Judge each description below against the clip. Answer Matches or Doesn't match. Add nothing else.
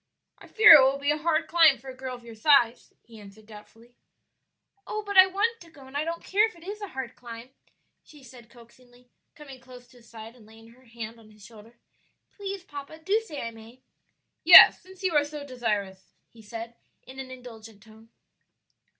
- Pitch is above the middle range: Matches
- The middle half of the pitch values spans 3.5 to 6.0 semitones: Matches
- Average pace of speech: Doesn't match